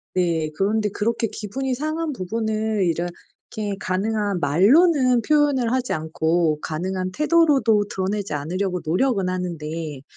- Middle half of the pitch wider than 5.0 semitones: Yes, wide, 5.6 semitones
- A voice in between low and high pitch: No, high, 200 Hz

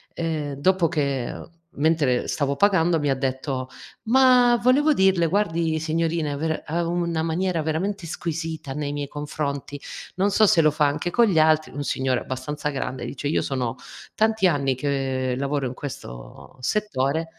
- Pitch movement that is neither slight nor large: Yes, average, 3.7 semitones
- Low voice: No, medium, 155 Hz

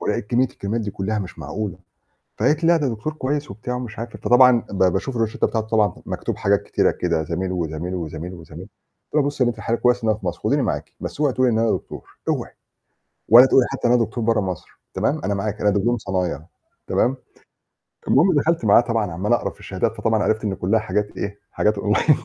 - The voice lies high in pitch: No, low, 110 Hz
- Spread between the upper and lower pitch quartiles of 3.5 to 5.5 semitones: Yes, average, 4.1 semitones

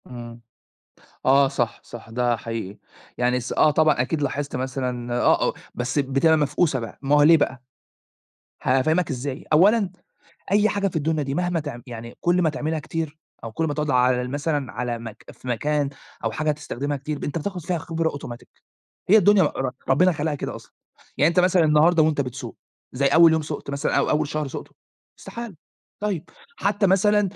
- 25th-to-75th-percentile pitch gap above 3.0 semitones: Yes, average, 4.3 semitones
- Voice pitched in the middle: Yes, medium, 145 Hz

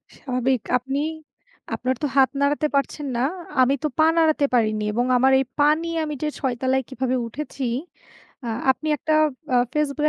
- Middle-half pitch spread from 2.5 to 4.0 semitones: Yes, average, 2.9 semitones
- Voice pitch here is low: No, very high, 270 Hz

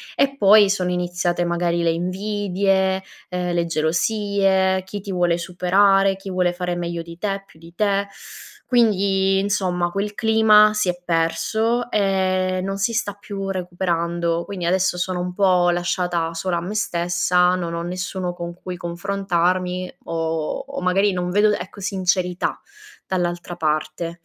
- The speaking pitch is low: No, medium, 185 Hz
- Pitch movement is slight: Yes, narrow, 2.1 semitones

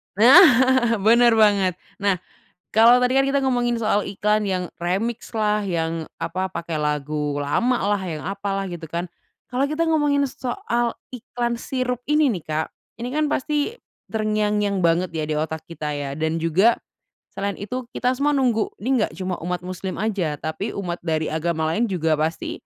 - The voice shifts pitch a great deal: Yes, wide, 6.5 semitones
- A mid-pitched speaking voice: No, high, 205 Hz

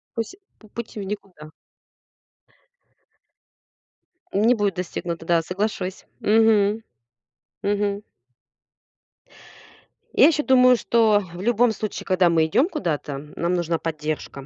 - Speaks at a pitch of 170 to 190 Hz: No, high, 200 Hz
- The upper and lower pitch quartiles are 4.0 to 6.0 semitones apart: Yes, average, 4.6 semitones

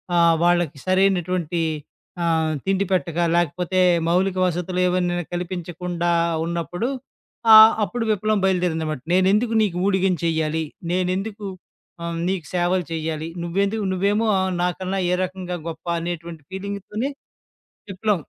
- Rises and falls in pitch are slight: Yes, narrow, 2.1 semitones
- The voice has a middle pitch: Yes, medium, 180 Hz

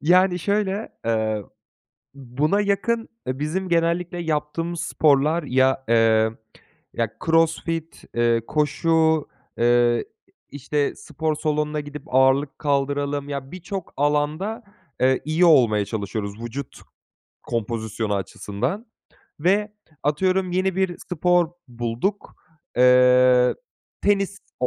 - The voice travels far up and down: Yes, wide, 5.7 semitones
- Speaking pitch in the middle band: Yes, medium, 150 Hz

